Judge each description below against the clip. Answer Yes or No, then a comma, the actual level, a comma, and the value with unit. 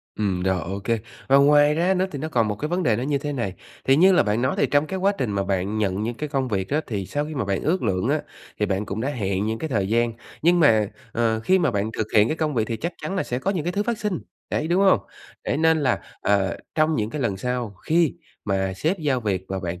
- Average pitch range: No, wide, 7.2 semitones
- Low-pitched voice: Yes, low, 125 Hz